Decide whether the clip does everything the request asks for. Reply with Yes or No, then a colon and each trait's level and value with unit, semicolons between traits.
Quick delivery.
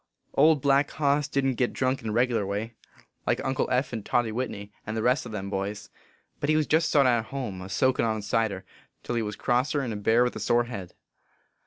Yes: fast, 225 wpm